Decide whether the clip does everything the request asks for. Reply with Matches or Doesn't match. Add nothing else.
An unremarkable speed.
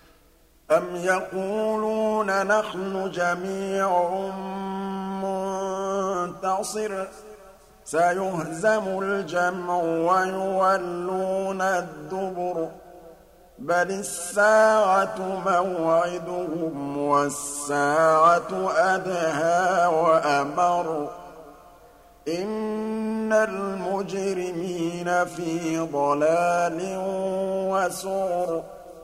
Doesn't match